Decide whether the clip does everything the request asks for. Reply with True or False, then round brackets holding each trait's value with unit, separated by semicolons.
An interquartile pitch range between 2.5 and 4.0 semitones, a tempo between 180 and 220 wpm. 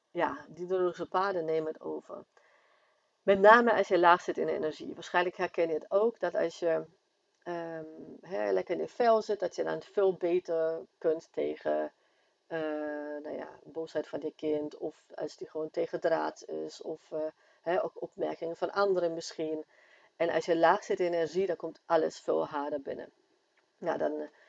True (2.8 semitones; 185 wpm)